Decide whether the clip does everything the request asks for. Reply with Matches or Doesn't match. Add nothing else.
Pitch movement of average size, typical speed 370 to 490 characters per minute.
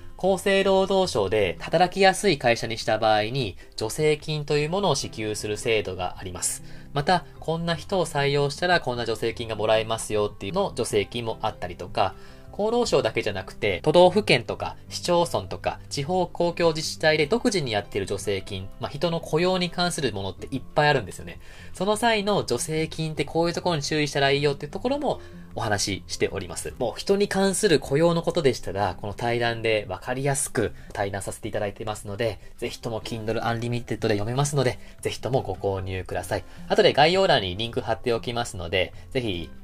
Doesn't match